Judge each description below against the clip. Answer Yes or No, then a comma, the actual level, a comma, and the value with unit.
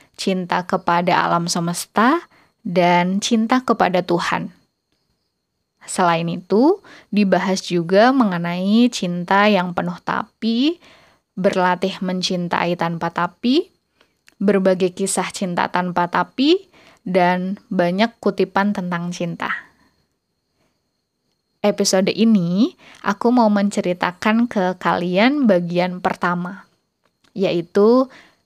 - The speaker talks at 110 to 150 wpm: No, slow, 85 wpm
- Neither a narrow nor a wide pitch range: Yes, average, 3.8 semitones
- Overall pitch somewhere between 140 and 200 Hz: Yes, high, 190 Hz